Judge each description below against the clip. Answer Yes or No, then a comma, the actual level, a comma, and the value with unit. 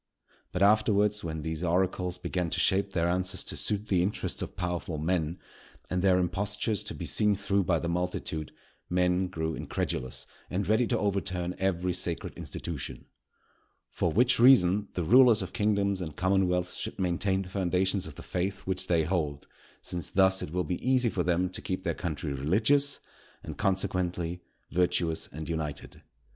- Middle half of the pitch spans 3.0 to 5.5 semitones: No, narrow, 2.4 semitones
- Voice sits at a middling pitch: No, very low, 90 Hz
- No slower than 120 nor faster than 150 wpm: No, average, 170 wpm